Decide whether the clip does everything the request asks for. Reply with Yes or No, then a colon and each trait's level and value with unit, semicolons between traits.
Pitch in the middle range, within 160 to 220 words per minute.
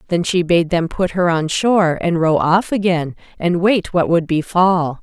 Yes: medium, 175 Hz; fast, 205 wpm